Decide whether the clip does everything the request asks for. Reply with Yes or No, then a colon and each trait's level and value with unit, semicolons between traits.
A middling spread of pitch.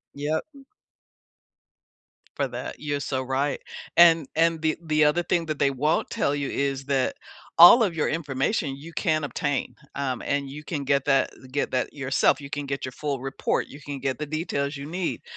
No: narrow, 2.2 semitones